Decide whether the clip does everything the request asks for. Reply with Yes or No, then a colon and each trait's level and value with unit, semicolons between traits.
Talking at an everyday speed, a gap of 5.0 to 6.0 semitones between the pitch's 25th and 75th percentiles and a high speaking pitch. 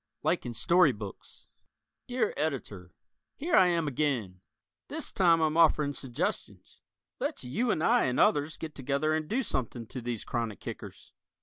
No: average, 155 wpm; wide, 5.5 semitones; medium, 145 Hz